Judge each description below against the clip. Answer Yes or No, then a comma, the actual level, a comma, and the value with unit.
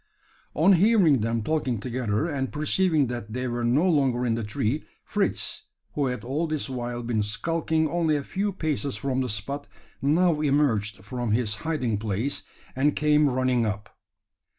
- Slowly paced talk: No, average, 165 wpm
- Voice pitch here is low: Yes, low, 130 Hz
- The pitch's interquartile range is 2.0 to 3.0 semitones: No, average, 4.7 semitones